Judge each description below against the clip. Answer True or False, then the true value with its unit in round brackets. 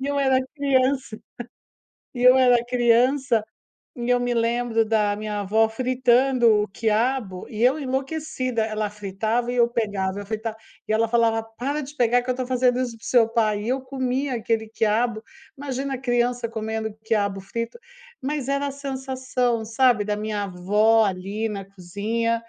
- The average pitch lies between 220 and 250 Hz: True (235 Hz)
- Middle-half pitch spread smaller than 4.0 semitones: True (3.0 semitones)